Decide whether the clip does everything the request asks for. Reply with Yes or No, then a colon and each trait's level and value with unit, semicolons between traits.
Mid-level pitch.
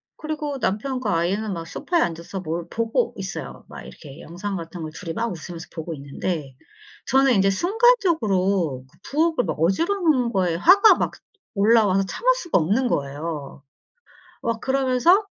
No: high, 200 Hz